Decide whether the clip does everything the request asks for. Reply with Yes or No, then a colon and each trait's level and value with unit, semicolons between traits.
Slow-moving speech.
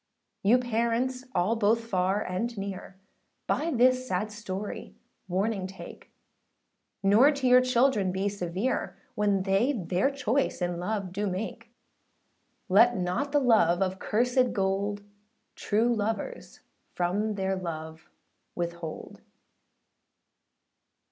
Yes: slow, 115 wpm